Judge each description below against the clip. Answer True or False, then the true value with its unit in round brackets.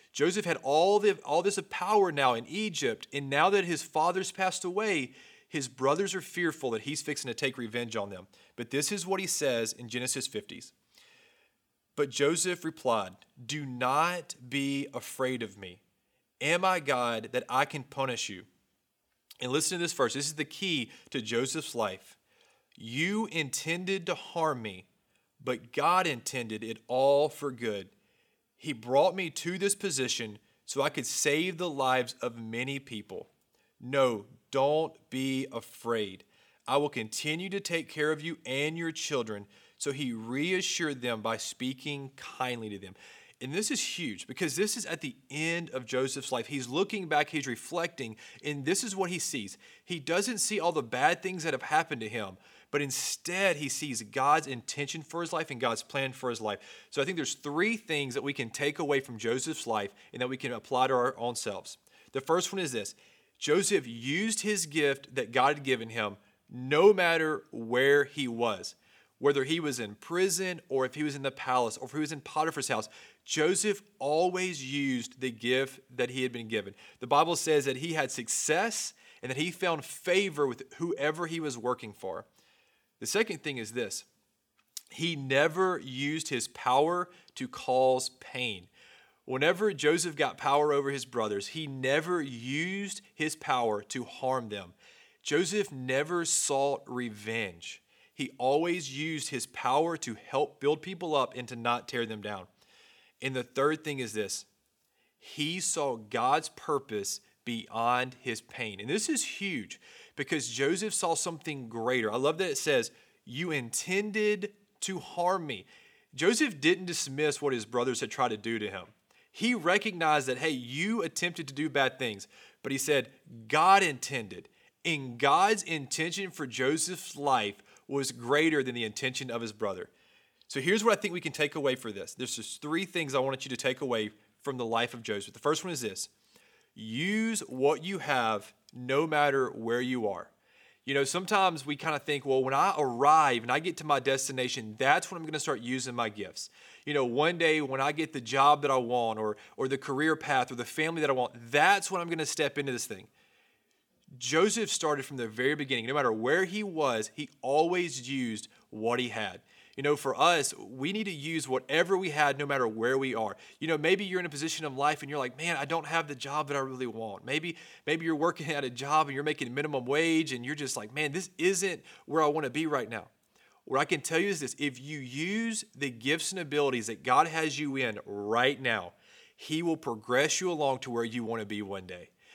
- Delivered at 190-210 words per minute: True (195 wpm)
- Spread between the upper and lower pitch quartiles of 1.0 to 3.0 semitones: False (4.8 semitones)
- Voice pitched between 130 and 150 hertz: True (140 Hz)